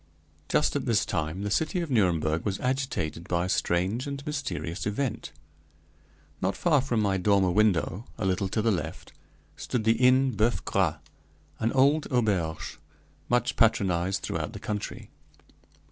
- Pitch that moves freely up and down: Yes, wide, 5.7 semitones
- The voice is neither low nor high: No, low, 105 Hz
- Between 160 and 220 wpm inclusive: No, average, 150 wpm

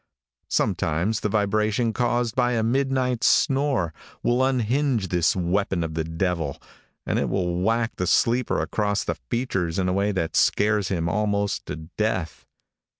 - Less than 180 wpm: Yes, average, 150 wpm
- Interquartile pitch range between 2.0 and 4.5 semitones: No, average, 5.1 semitones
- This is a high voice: No, low, 105 Hz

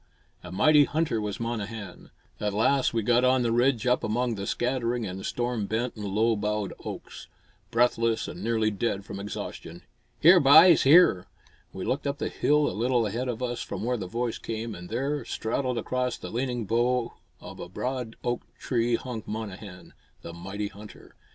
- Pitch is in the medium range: No, low, 115 Hz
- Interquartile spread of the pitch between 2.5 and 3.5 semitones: Yes, average, 3.1 semitones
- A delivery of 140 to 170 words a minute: No, average, 180 wpm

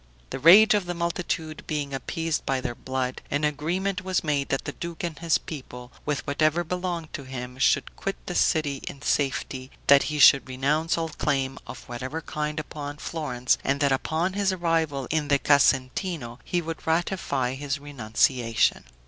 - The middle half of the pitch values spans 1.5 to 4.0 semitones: Yes, average, 3.7 semitones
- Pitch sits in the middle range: Yes, medium, 150 Hz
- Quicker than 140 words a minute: Yes, average, 175 wpm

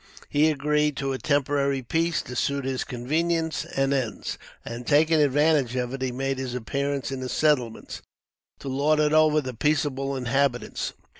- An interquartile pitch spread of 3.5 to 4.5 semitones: No, narrow, 2.6 semitones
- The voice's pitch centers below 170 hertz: Yes, medium, 140 Hz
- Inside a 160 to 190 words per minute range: Yes, average, 170 wpm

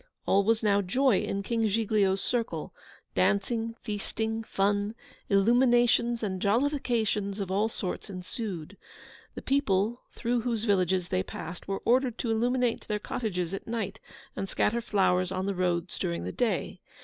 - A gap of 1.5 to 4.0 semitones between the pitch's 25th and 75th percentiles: Yes, average, 3.2 semitones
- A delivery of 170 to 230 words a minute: No, average, 150 wpm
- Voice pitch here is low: No, high, 210 Hz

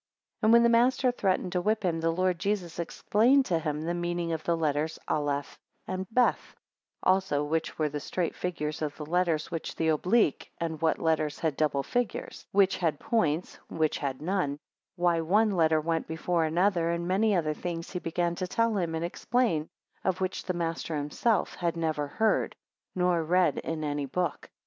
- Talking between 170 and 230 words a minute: Yes, average, 190 wpm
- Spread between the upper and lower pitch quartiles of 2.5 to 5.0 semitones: Yes, average, 3.0 semitones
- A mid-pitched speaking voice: Yes, medium, 170 Hz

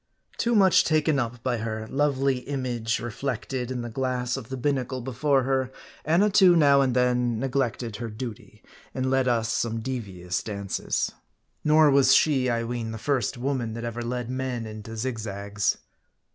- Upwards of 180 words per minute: No, average, 165 wpm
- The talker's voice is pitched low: Yes, low, 125 Hz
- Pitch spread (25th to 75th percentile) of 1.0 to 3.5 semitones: Yes, average, 2.9 semitones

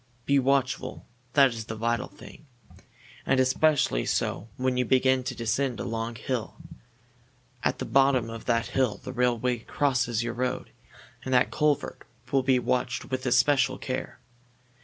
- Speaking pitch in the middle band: No, low, 125 Hz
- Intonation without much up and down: Yes, narrow, 2.2 semitones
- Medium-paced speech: Yes, average, 155 wpm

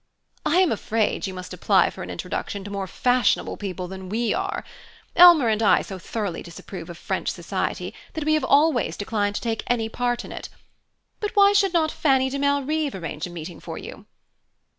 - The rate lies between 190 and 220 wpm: Yes, average, 195 wpm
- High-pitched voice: Yes, high, 230 Hz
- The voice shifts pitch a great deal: Yes, wide, 7.8 semitones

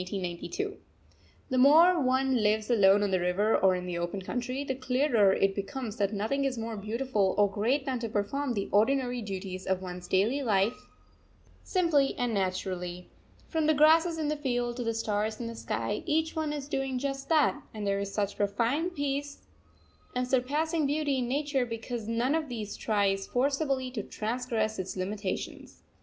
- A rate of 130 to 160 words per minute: No, average, 180 wpm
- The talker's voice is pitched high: Yes, high, 240 Hz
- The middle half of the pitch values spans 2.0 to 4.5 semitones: No, average, 5.3 semitones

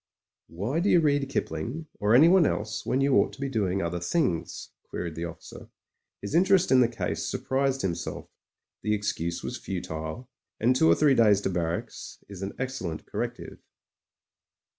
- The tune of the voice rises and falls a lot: Yes, wide, 7.8 semitones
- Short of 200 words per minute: Yes, average, 170 wpm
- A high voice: No, low, 105 Hz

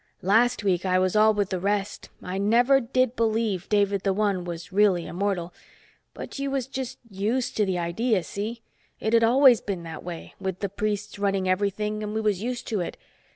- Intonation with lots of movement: No, average, 3.3 semitones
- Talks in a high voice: Yes, high, 205 Hz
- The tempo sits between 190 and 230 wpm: Yes, average, 195 wpm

